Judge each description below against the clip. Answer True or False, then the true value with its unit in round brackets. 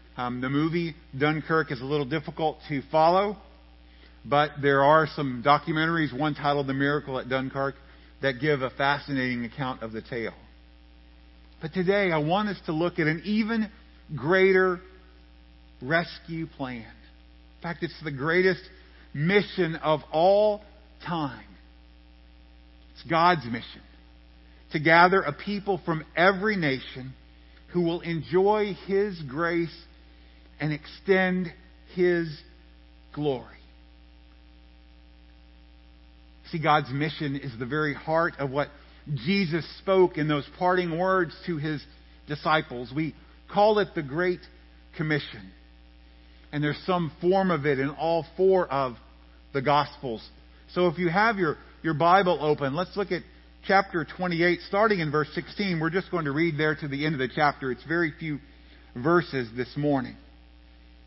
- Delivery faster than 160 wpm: False (140 wpm)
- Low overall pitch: False (145 Hz)